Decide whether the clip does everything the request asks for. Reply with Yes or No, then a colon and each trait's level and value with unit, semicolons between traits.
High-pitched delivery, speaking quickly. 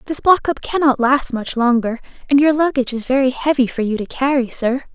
Yes: very high, 260 Hz; fast, 220 wpm